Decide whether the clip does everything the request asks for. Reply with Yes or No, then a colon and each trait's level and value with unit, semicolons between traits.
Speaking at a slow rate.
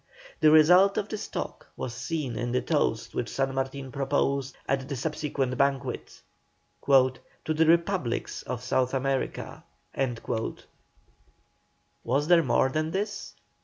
Yes: slow, 130 wpm